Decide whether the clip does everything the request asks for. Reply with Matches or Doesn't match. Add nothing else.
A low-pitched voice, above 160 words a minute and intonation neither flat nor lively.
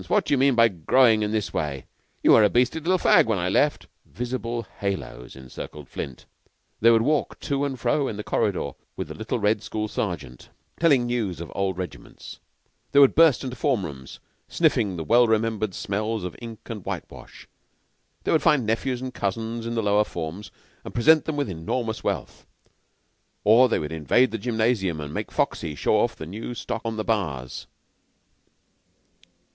Matches